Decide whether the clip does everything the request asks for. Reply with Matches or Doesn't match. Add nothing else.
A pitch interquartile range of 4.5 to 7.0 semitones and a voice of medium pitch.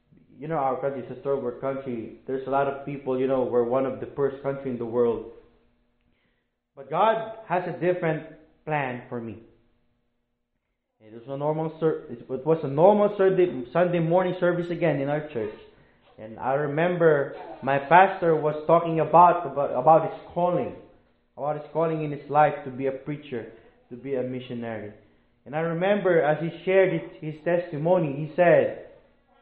Matches